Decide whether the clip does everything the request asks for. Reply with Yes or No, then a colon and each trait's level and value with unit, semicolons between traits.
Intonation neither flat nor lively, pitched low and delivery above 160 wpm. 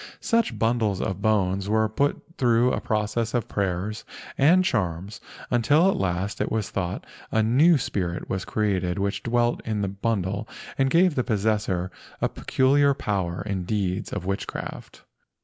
No: average, 3.9 semitones; low, 105 Hz; average, 155 wpm